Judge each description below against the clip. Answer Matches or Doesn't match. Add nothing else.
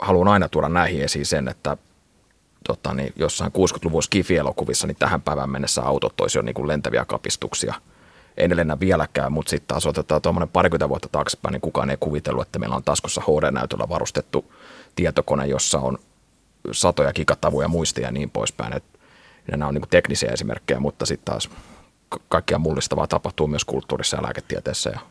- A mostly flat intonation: Doesn't match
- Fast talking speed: Matches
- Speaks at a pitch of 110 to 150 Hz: Doesn't match